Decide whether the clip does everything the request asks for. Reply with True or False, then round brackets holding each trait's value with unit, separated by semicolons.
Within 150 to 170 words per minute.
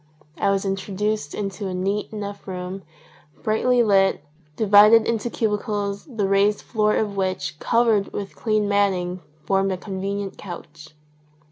False (140 wpm)